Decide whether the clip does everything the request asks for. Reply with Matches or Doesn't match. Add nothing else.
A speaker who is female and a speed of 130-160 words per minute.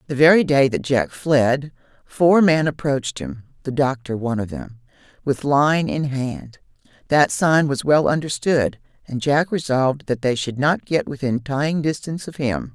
Doesn't match